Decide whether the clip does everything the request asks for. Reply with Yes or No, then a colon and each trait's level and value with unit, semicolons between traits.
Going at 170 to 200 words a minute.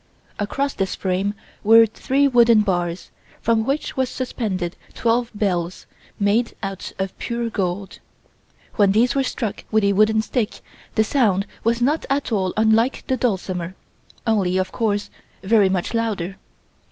No: average, 145 wpm